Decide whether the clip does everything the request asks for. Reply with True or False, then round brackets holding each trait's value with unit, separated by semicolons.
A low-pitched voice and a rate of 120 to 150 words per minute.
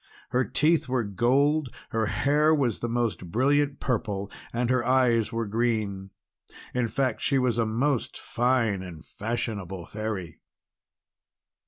True (120 Hz; 140 wpm)